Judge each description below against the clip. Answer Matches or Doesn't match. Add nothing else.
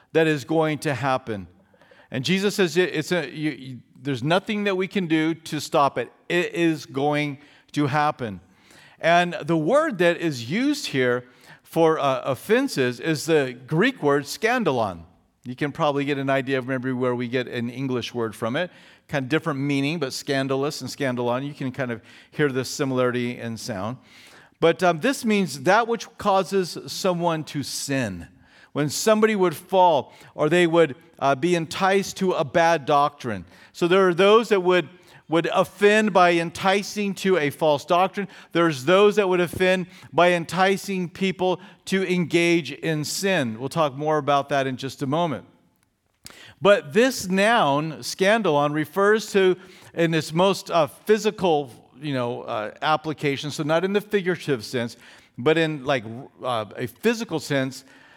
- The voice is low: Doesn't match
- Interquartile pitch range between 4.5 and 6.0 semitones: Matches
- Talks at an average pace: Matches